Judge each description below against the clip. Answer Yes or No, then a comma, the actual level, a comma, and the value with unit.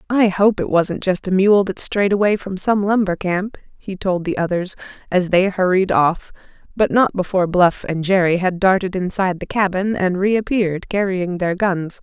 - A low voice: No, high, 190 Hz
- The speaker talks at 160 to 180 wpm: No, average, 190 wpm